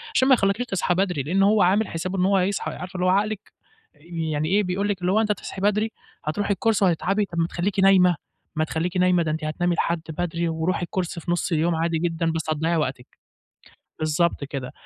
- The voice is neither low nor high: Yes, medium, 180 Hz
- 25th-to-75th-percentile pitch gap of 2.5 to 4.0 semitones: Yes, average, 3.2 semitones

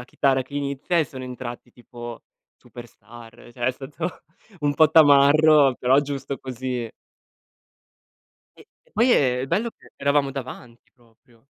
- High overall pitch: No, low, 135 Hz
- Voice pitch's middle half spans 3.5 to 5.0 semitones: No, average, 2.8 semitones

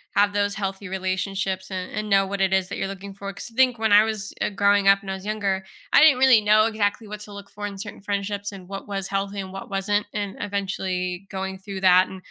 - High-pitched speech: Yes, high, 200 Hz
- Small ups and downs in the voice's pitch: Yes, narrow, 1.3 semitones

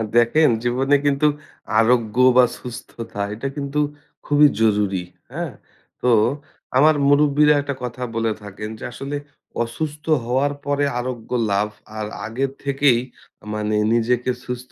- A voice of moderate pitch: No, low, 125 Hz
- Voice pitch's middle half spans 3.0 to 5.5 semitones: Yes, average, 4.0 semitones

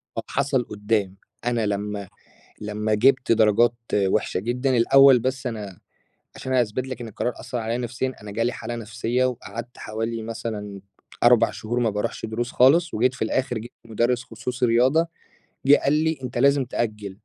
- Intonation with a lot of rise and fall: No, average, 2.9 semitones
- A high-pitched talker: No, low, 120 Hz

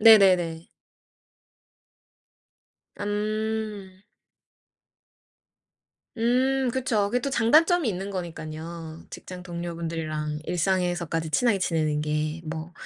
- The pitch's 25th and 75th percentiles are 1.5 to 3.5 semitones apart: No, average, 5.1 semitones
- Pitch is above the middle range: No, medium, 180 Hz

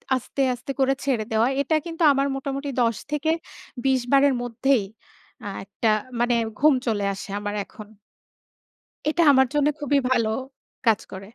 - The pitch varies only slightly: No, average, 3.8 semitones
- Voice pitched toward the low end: No, very high, 265 Hz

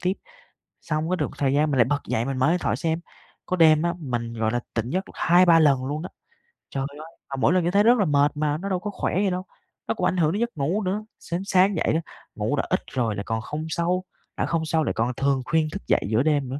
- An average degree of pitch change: Yes, average, 4.9 semitones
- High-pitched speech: No, medium, 155 Hz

